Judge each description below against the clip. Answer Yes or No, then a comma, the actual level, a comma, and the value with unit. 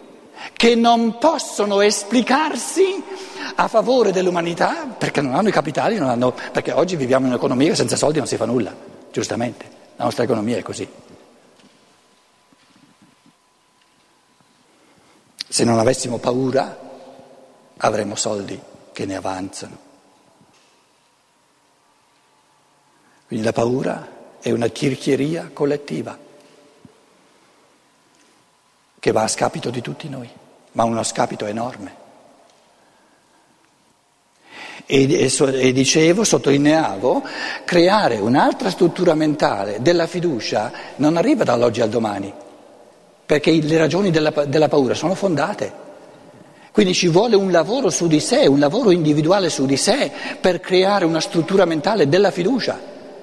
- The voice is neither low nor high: Yes, medium, 160 Hz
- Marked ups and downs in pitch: Yes, wide, 6.6 semitones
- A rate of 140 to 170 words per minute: No, slow, 115 wpm